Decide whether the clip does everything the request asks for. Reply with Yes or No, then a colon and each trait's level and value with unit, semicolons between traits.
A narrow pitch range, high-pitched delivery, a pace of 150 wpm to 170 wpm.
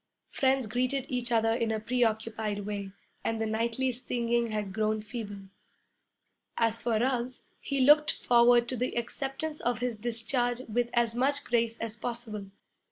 Yes: narrow, 2.1 semitones; high, 235 Hz; average, 155 wpm